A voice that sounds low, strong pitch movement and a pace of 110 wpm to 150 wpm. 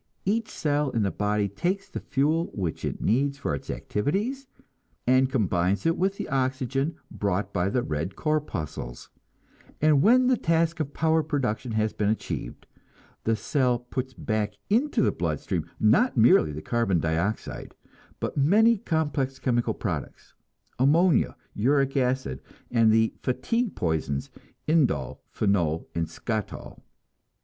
Yes: low, 130 Hz; wide, 7.2 semitones; average, 140 wpm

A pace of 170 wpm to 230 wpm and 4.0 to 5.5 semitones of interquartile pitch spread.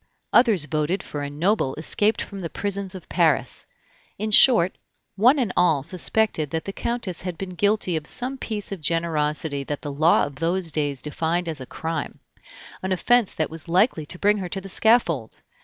Yes: average, 190 wpm; average, 4.7 semitones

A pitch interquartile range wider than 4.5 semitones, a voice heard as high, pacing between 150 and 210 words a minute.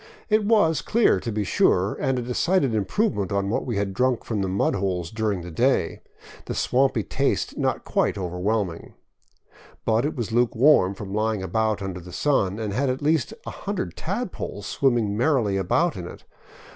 No: average, 4.9 semitones; low, 110 Hz; average, 185 wpm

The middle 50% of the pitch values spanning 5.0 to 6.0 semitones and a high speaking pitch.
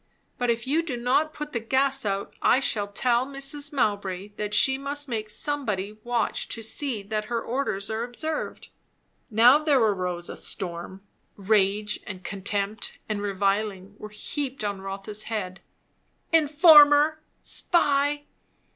Yes: wide, 5.4 semitones; high, 225 Hz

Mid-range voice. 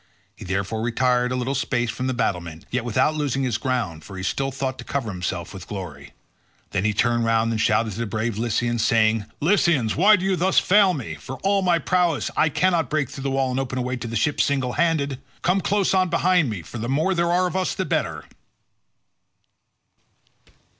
No: low, 125 Hz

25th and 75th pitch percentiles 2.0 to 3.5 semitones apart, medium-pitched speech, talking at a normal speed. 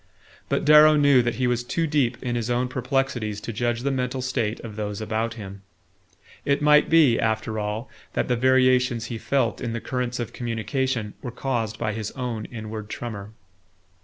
No: average, 2.8 semitones; low, 120 Hz; average, 185 wpm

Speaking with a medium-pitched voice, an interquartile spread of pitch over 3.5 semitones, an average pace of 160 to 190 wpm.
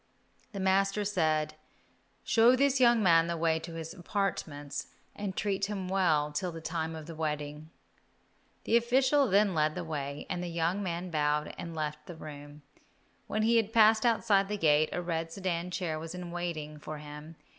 Yes: medium, 170 Hz; average, 4.3 semitones; average, 185 wpm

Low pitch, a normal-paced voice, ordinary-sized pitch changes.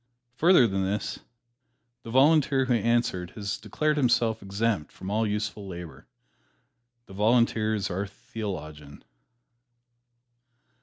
No: low, 105 Hz; slow, 110 wpm; average, 3.6 semitones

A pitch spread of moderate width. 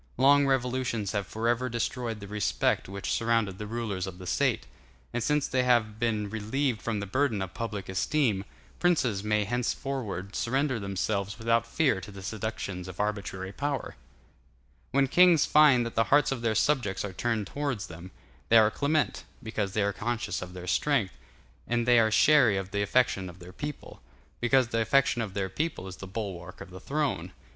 Yes: average, 4.5 semitones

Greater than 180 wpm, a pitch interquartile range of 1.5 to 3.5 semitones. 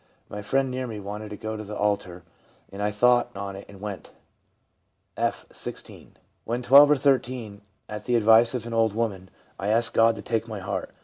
Yes: fast, 205 wpm; average, 2.7 semitones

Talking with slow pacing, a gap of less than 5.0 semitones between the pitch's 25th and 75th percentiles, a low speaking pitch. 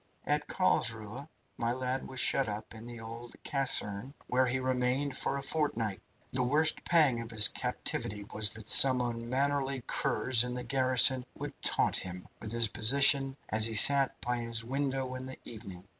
No: average, 175 wpm; average, 2.9 semitones; low, 125 Hz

